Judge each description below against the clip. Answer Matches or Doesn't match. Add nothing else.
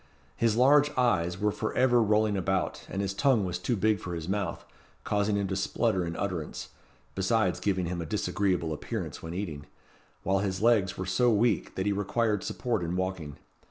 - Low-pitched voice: Matches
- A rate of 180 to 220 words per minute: Matches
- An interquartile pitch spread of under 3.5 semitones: Matches